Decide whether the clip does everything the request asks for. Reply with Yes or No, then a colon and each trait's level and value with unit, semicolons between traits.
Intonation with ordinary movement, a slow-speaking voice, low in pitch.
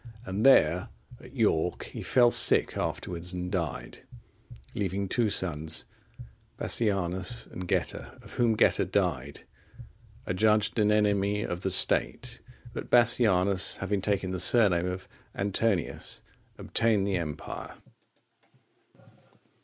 Yes: average, 3.1 semitones; slow, 115 wpm; very low, 95 Hz